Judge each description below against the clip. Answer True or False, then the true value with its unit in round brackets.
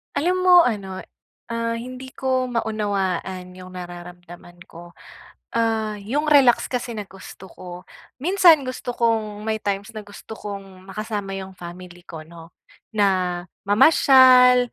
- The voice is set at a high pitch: True (210 Hz)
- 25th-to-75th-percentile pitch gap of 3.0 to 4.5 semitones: False (5.0 semitones)